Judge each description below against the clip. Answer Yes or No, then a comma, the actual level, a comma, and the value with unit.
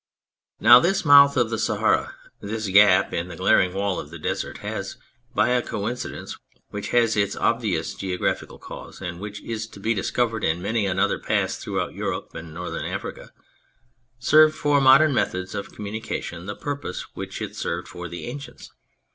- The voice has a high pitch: No, low, 105 Hz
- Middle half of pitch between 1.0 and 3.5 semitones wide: No, average, 4.8 semitones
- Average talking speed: Yes, average, 170 wpm